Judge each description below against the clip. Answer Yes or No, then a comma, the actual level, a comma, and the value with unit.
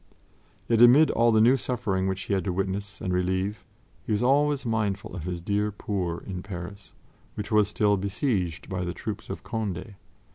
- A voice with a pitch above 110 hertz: No, low, 100 Hz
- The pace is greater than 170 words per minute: Yes, average, 185 wpm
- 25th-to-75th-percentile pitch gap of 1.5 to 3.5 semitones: Yes, average, 3.0 semitones